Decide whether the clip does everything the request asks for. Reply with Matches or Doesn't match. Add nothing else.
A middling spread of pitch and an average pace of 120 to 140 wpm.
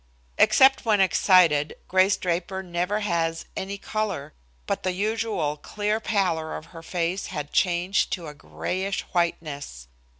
Matches